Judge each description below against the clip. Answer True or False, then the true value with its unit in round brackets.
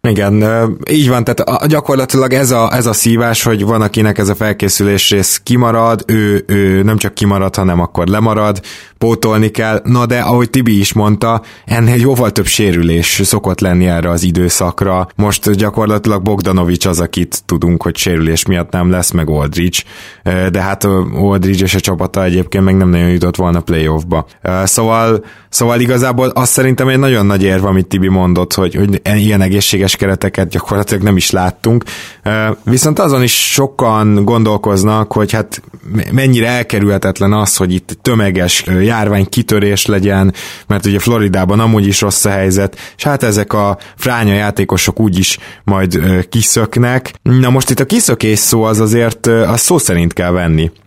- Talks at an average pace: False (165 wpm)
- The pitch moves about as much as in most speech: True (3.2 semitones)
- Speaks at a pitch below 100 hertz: False (105 Hz)